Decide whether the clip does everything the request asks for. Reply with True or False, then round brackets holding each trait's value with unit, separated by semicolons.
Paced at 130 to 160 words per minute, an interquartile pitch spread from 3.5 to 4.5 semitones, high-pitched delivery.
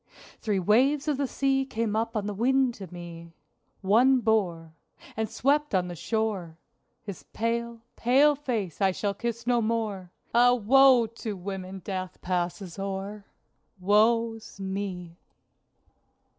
True (135 wpm; 3.8 semitones; 215 Hz)